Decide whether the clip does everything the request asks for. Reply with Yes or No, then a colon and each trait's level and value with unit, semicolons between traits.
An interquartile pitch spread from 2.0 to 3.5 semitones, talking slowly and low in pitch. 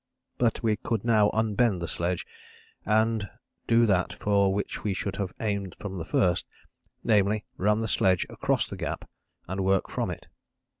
No: narrow, 2.4 semitones; average, 165 wpm; low, 100 Hz